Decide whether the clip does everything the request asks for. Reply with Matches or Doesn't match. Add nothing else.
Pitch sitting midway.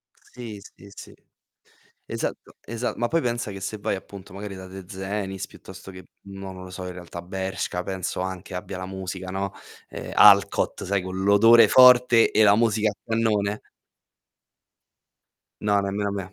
Doesn't match